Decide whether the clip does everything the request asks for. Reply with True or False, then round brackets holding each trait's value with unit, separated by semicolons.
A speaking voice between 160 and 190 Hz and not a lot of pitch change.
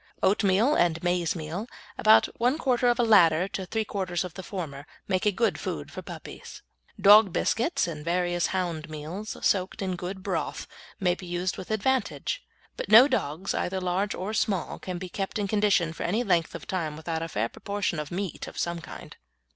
False (185 Hz; 3.3 semitones)